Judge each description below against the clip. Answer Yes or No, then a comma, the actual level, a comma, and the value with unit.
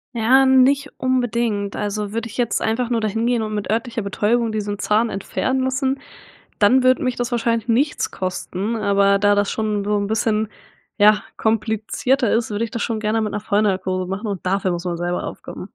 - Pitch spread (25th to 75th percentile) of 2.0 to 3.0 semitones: Yes, average, 2.7 semitones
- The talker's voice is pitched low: No, high, 220 Hz